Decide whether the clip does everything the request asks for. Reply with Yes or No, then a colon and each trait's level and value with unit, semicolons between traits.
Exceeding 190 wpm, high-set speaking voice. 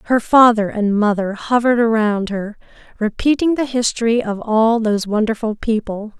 No: average, 145 wpm; high, 225 Hz